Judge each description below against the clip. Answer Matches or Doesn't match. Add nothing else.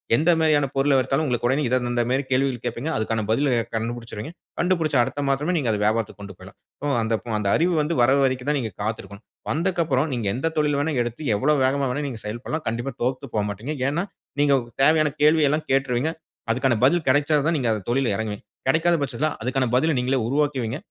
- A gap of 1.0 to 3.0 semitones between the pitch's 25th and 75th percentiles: Doesn't match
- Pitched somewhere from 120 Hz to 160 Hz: Matches